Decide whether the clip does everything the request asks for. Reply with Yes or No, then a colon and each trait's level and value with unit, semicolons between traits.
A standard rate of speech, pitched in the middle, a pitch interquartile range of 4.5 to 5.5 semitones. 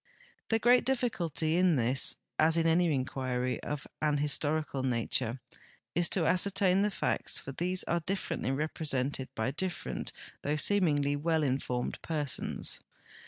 Yes: average, 145 wpm; medium, 155 Hz; average, 4.9 semitones